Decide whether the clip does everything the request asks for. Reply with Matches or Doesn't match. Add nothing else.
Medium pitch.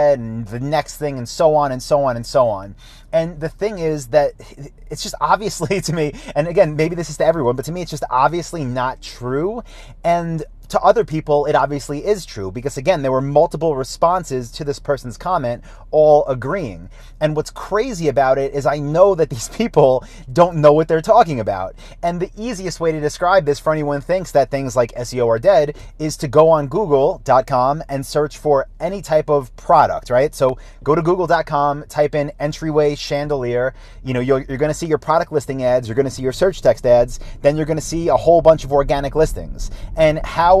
Matches